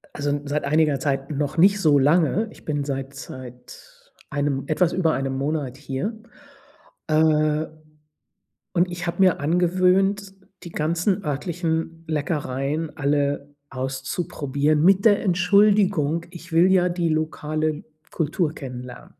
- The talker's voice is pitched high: No, medium, 155 Hz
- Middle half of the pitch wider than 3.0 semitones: Yes, average, 3.8 semitones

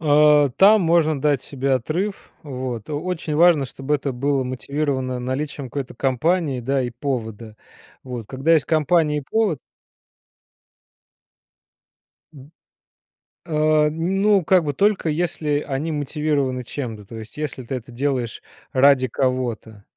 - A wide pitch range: No, average, 3.3 semitones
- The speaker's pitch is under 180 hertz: Yes, medium, 140 Hz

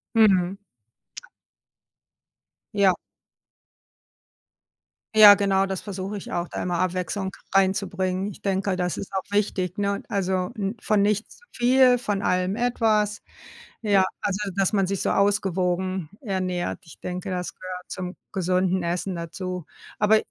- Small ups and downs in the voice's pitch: Yes, narrow, 1.9 semitones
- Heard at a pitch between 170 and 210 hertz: Yes, high, 190 Hz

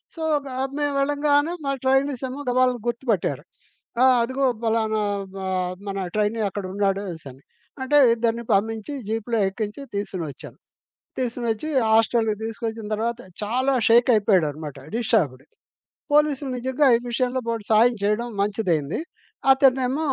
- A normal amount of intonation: Yes, average, 4.0 semitones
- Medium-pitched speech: No, high, 230 Hz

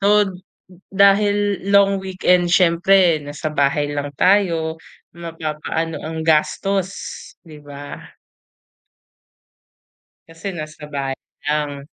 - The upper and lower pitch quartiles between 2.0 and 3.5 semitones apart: No, average, 4.3 semitones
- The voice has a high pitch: No, medium, 165 Hz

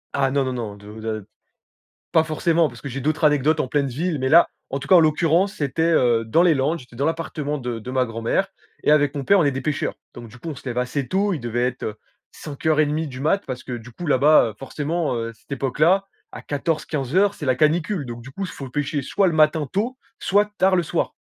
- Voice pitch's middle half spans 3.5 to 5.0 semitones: Yes, average, 4.3 semitones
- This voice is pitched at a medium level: Yes, medium, 145 Hz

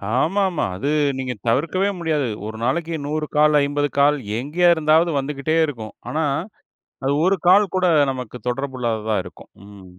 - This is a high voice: No, medium, 145 Hz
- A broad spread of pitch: No, average, 4.3 semitones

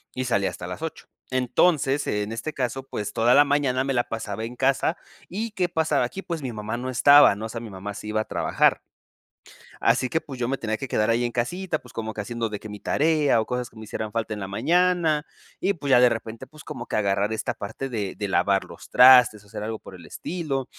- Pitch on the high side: No, low, 120 Hz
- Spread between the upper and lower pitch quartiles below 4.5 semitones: No, average, 4.8 semitones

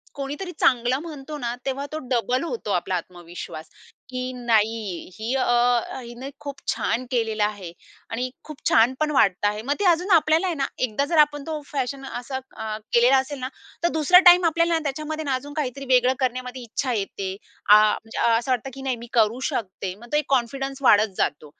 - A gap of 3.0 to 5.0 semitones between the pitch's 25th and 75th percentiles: Yes, average, 4.1 semitones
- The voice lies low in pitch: No, very high, 255 Hz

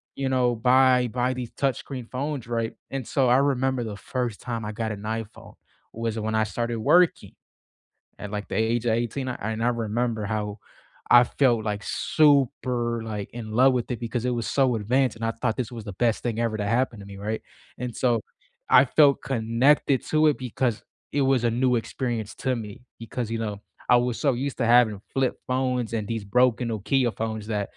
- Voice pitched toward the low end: Yes, low, 120 Hz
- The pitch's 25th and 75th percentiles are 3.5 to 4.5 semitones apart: No, narrow, 2.5 semitones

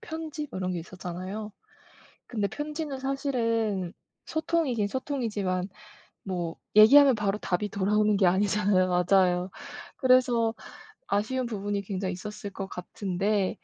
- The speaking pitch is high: Yes, high, 210 Hz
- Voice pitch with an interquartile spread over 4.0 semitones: Yes, average, 5.3 semitones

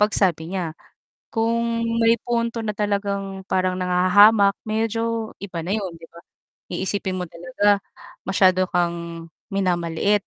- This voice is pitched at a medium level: No, high, 195 Hz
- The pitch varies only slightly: No, average, 3.4 semitones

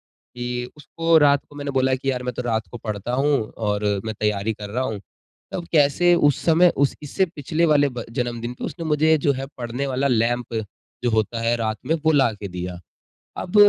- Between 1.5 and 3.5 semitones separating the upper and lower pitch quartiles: No, average, 4.2 semitones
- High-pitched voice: No, low, 125 Hz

